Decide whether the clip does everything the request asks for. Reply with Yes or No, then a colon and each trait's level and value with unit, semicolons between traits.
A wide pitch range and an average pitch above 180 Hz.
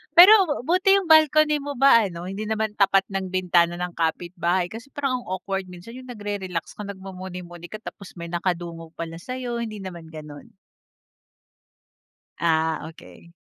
Yes: wide, 5.7 semitones; high, 190 Hz